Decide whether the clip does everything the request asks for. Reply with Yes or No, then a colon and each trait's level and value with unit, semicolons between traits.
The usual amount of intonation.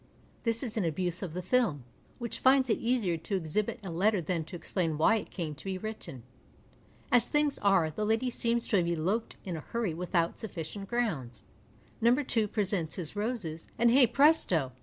No: wide, 5.9 semitones